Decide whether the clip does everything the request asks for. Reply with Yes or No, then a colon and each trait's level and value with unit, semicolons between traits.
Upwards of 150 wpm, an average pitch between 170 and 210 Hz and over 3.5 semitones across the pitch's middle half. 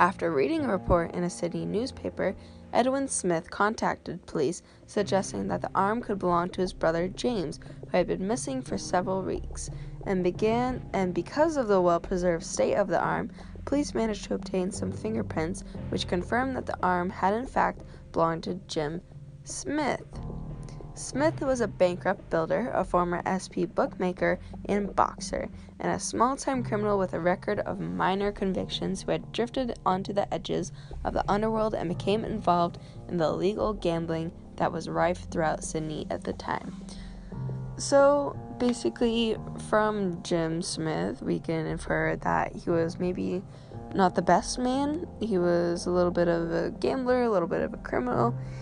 Yes: average, 165 wpm; medium, 185 Hz; average, 3.9 semitones